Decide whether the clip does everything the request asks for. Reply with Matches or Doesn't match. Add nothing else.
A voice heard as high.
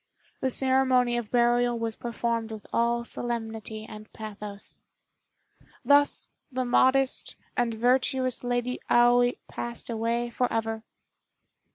Matches